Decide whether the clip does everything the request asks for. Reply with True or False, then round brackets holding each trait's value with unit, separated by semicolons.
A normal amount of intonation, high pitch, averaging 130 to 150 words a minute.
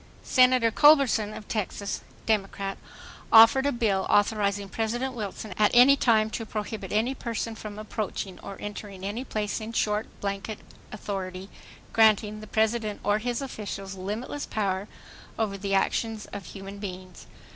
False (2.3 semitones; 215 Hz; 140 wpm)